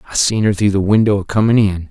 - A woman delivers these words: No, male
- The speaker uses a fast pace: Yes, fast, 285 wpm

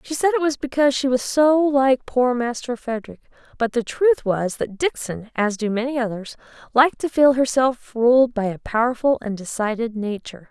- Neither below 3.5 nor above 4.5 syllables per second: No, 5.1 syllables/s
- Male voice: No, female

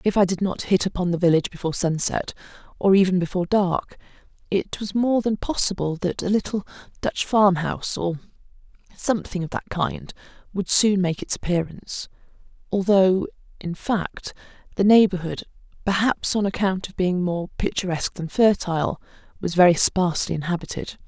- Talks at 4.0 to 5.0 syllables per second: Yes, 4.6 syllables/s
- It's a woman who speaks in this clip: Yes, female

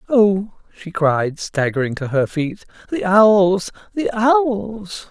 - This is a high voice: Yes, high, 195 Hz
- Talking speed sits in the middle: No, slow, 130 wpm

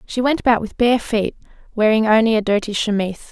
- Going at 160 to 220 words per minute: Yes, average, 200 wpm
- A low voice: No, high, 220 Hz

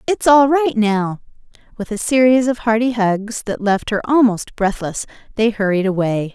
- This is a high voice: Yes, high, 220 Hz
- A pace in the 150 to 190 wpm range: Yes, average, 170 wpm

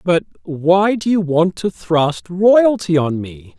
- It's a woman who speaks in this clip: No, male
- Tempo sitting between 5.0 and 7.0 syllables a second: No, 3.3 syllables/s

